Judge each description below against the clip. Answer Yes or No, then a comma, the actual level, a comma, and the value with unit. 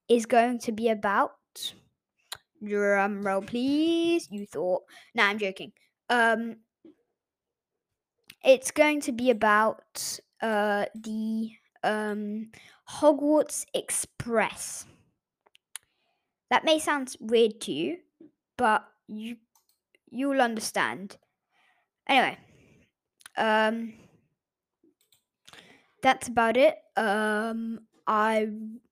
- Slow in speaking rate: Yes, slow, 85 wpm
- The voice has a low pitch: No, high, 230 Hz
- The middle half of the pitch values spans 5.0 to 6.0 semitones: Yes, wide, 5.5 semitones